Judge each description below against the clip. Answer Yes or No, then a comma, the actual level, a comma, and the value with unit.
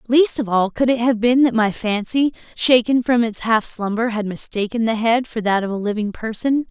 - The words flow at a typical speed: No, fast, 225 wpm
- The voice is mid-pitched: No, high, 230 Hz